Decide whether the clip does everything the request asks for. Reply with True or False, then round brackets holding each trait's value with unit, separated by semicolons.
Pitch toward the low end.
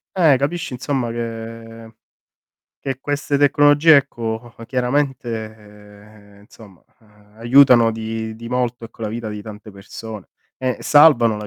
True (115 Hz)